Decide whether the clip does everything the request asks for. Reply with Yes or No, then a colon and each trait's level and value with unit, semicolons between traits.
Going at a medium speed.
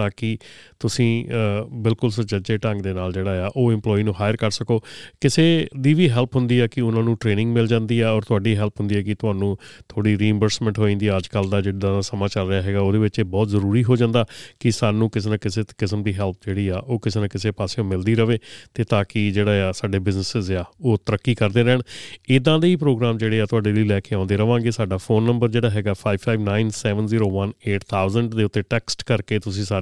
No: fast, 210 wpm